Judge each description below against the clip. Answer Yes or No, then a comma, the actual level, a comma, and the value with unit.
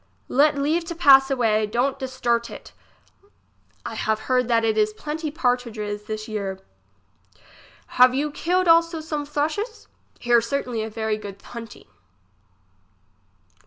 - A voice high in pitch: Yes, very high, 250 Hz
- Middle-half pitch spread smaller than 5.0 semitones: No, average, 5.3 semitones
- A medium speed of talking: No, slow, 130 wpm